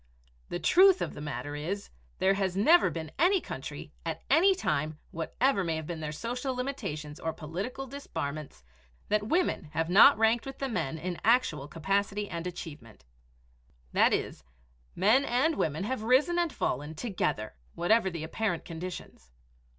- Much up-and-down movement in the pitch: Yes, wide, 8.0 semitones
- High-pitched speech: Yes, high, 195 Hz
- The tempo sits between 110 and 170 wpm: Yes, average, 160 wpm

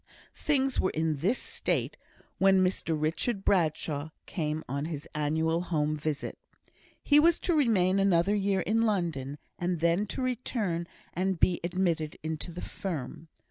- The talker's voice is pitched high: No, medium, 175 Hz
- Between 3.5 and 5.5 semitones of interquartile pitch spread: Yes, average, 4.0 semitones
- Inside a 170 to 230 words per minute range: No, average, 145 wpm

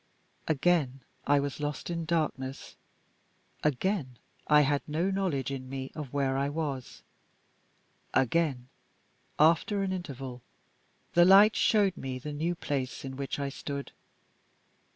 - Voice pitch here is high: No, medium, 145 Hz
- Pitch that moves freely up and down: No, average, 4.0 semitones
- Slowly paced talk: Yes, slow, 130 wpm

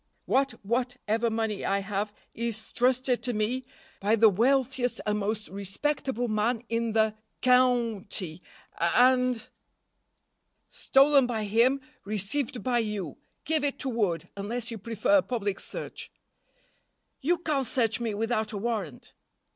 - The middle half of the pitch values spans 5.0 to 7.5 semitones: No, average, 3.2 semitones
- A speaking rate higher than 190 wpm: No, average, 140 wpm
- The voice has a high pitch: Yes, high, 230 Hz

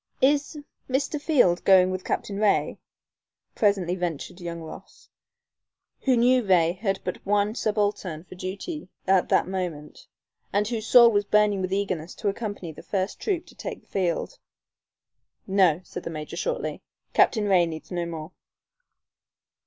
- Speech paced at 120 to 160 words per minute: Yes, average, 150 wpm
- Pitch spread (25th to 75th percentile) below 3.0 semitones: No, average, 3.6 semitones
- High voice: Yes, high, 195 Hz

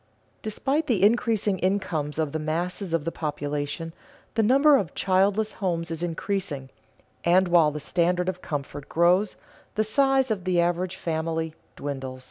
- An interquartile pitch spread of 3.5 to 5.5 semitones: Yes, average, 4.3 semitones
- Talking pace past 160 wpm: No, average, 150 wpm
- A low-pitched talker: No, medium, 175 Hz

